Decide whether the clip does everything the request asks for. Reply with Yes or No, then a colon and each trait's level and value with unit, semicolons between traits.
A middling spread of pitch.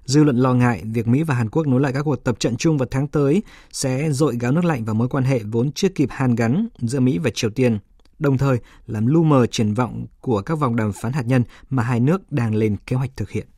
Yes: average, 3.9 semitones